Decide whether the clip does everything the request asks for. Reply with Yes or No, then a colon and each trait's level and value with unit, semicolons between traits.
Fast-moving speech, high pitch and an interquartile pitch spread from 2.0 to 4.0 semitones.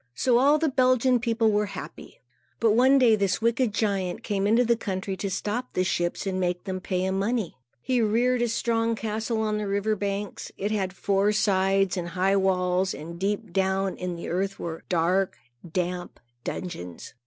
No: average, 185 wpm; high, 200 Hz; average, 3.4 semitones